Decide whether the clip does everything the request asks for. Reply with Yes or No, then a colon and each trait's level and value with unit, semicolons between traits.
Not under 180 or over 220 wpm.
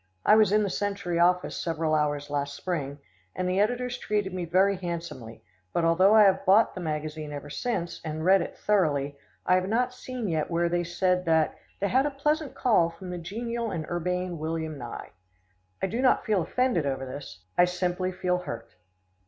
Yes: average, 195 wpm